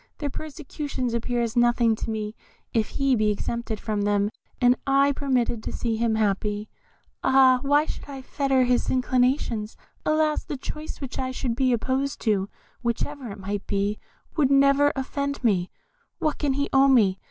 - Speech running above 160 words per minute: Yes, average, 170 wpm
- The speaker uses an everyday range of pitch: Yes, average, 4.0 semitones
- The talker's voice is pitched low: No, very high, 250 Hz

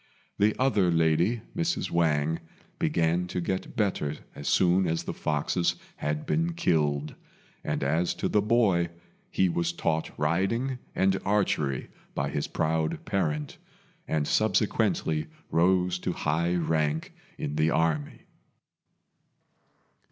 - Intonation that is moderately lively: Yes, average, 3.6 semitones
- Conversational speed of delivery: No, slow, 120 wpm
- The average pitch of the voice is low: Yes, very low, 85 Hz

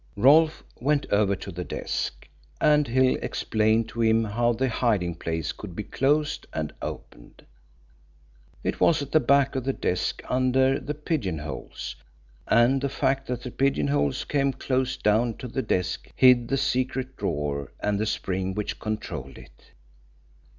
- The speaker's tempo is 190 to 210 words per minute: No, average, 155 wpm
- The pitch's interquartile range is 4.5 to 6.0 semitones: Yes, average, 5.2 semitones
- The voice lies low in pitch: Yes, low, 120 Hz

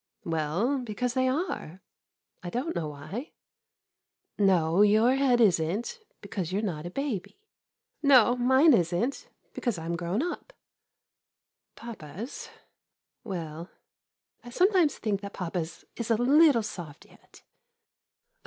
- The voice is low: No, high, 215 Hz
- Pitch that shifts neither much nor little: No, wide, 6.9 semitones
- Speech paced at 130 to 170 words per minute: Yes, average, 145 wpm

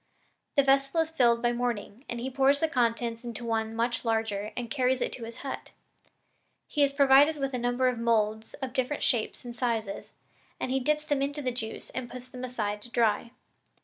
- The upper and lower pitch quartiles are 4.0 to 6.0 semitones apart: No, average, 2.8 semitones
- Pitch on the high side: Yes, high, 245 Hz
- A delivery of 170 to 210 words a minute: Yes, fast, 205 wpm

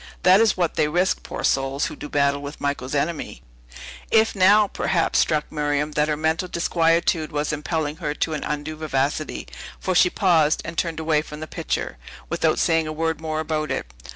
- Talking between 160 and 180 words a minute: No, average, 190 wpm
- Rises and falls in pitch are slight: Yes, narrow, 2.1 semitones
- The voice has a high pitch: No, medium, 155 Hz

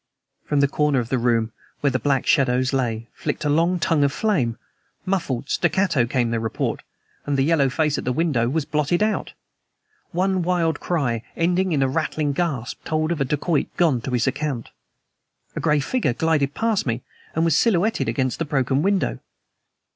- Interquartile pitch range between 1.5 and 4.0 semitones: No, average, 4.6 semitones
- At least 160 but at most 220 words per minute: Yes, average, 185 wpm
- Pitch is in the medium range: Yes, medium, 145 Hz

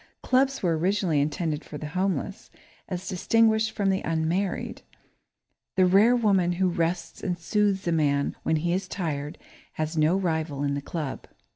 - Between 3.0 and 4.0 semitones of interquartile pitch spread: Yes, average, 3.7 semitones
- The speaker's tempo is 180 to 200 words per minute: No, average, 160 wpm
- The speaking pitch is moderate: Yes, medium, 175 Hz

